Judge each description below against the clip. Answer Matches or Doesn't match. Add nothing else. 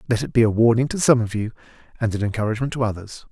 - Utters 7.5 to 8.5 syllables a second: Matches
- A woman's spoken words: Doesn't match